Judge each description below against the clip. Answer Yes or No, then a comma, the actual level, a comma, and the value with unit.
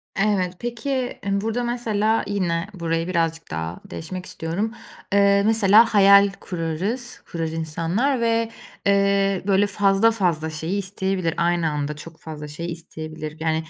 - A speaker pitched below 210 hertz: Yes, high, 190 Hz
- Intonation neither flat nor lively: Yes, average, 4.0 semitones